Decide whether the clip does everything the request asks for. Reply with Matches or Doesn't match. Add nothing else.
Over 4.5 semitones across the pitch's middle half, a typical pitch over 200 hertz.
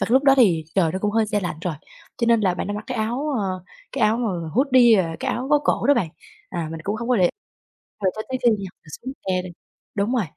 Matches